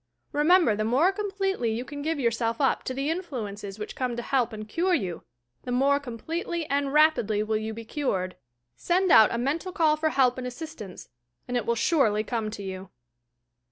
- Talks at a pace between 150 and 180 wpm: No, average, 190 wpm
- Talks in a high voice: Yes, very high, 250 Hz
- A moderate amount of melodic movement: No, wide, 6.1 semitones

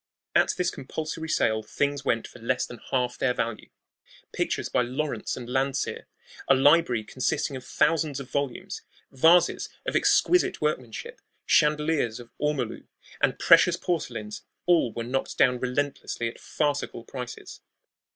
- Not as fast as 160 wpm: Yes, average, 140 wpm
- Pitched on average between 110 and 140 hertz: Yes, low, 135 Hz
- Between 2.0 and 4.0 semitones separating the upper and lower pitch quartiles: Yes, average, 3.7 semitones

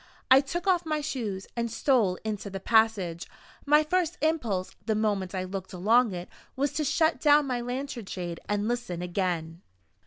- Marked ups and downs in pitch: Yes, wide, 7.1 semitones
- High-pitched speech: Yes, high, 225 Hz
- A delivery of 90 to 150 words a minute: No, average, 175 wpm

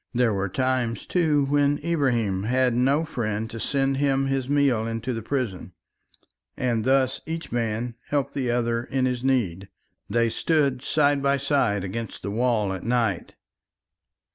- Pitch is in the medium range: No, low, 125 Hz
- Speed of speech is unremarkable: Yes, average, 155 wpm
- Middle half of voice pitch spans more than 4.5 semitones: No, average, 3.5 semitones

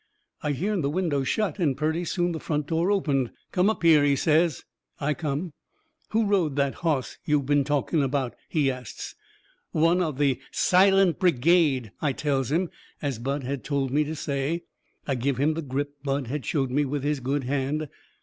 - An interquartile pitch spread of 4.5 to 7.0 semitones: No, average, 3.3 semitones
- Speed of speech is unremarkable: Yes, average, 190 wpm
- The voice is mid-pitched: Yes, medium, 145 Hz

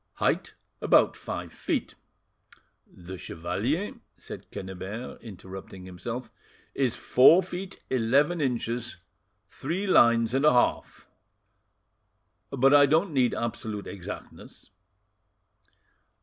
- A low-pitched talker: Yes, low, 120 Hz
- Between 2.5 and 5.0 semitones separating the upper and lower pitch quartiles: No, wide, 5.6 semitones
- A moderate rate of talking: No, slow, 95 wpm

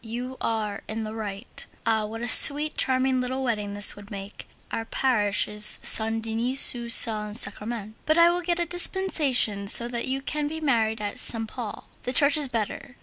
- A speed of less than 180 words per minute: No, average, 195 wpm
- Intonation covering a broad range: No, average, 3.8 semitones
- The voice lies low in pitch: No, high, 230 Hz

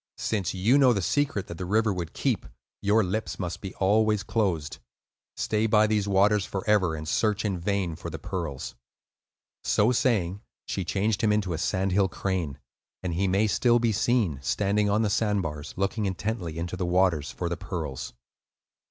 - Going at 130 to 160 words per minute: No, average, 180 wpm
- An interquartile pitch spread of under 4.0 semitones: Yes, average, 3.3 semitones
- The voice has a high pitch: No, low, 100 Hz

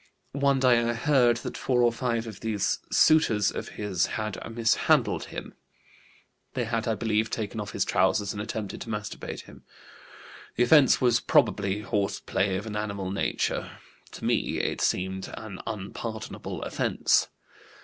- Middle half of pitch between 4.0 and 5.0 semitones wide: No, average, 2.7 semitones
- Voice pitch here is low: Yes, low, 110 Hz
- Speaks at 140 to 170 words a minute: Yes, average, 155 wpm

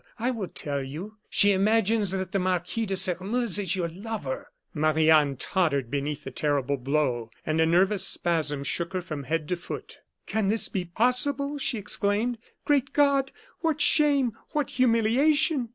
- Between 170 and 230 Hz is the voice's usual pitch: Yes, high, 190 Hz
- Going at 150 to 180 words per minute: Yes, average, 165 wpm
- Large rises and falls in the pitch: Yes, wide, 7.1 semitones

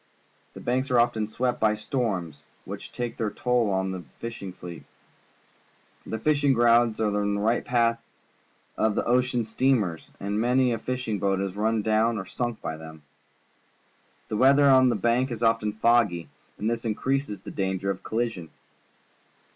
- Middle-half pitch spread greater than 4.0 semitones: No, average, 3.2 semitones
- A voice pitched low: Yes, low, 115 Hz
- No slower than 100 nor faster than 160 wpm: No, average, 170 wpm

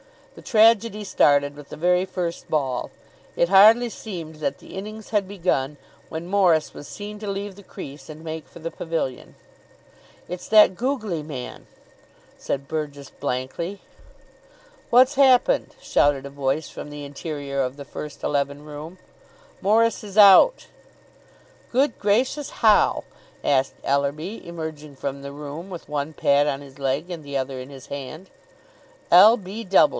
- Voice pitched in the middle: Yes, medium, 160 Hz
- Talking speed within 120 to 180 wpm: Yes, average, 150 wpm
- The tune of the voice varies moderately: No, wide, 6.1 semitones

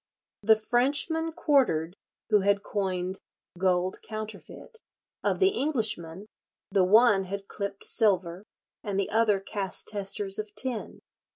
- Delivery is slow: Yes, slow, 120 wpm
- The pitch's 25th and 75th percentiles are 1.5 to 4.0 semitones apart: Yes, average, 2.9 semitones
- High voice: Yes, high, 205 Hz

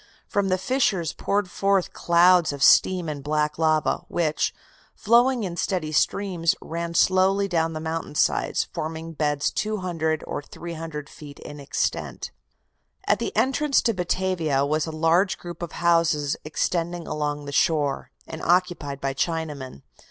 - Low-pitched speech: No, medium, 165 Hz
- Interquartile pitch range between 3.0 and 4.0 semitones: Yes, average, 3.3 semitones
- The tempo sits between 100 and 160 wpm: Yes, average, 145 wpm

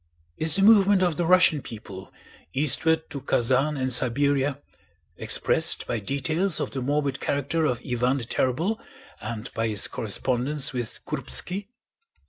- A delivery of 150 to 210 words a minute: No, average, 140 wpm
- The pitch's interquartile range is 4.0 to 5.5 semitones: Yes, average, 4.6 semitones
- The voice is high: No, medium, 140 Hz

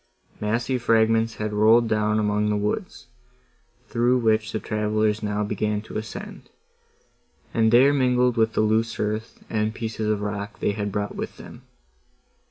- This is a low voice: Yes, low, 110 Hz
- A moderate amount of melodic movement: No, narrow, 1.3 semitones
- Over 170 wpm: No, average, 155 wpm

